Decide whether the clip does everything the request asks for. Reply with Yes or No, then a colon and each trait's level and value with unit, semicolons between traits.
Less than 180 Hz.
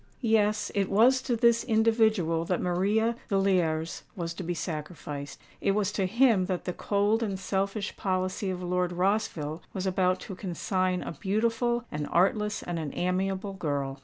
No: high, 190 Hz